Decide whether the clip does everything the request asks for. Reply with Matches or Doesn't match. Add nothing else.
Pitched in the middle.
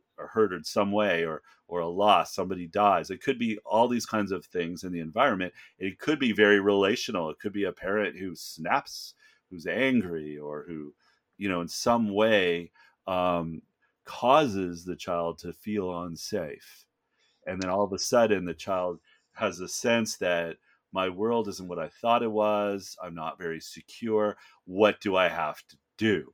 Doesn't match